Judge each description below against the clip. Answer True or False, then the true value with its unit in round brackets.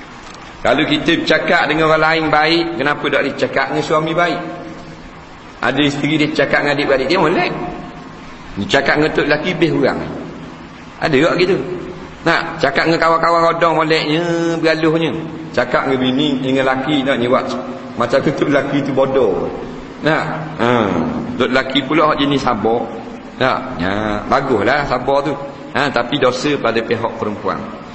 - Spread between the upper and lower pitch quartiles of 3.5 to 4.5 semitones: True (3.8 semitones)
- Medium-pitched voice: True (145 Hz)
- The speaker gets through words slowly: False (155 wpm)